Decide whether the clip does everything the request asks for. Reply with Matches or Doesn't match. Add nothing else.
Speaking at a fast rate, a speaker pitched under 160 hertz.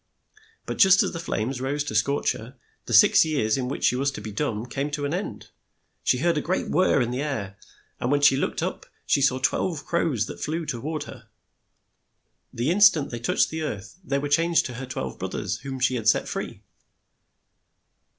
Matches